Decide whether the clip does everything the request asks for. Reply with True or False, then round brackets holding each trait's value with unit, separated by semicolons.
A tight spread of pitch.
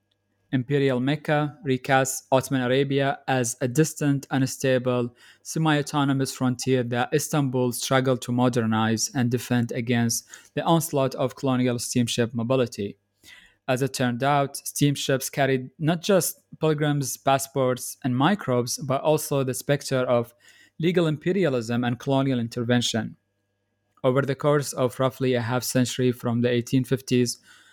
True (2.3 semitones)